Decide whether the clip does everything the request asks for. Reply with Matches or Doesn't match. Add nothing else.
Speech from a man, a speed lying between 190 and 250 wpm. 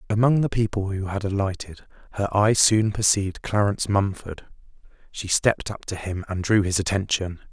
Doesn't match